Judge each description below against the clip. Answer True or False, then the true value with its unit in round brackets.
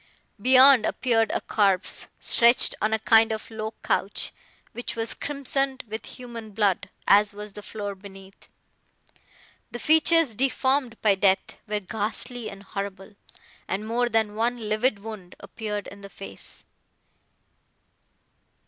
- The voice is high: True (220 Hz)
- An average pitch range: True (3.0 semitones)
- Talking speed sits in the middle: False (130 wpm)